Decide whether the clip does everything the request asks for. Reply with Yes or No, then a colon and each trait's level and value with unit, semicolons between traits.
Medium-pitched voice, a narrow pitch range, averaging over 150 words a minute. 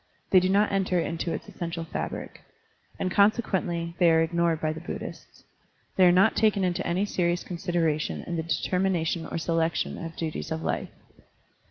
Yes: medium, 170 Hz; narrow, 2.1 semitones; average, 175 wpm